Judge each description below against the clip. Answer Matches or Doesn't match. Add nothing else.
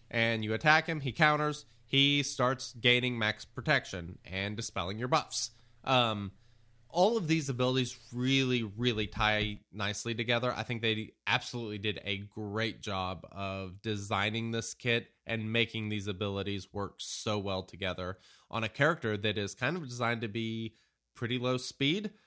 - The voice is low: Matches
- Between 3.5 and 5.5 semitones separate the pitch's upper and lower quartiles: Doesn't match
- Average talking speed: Matches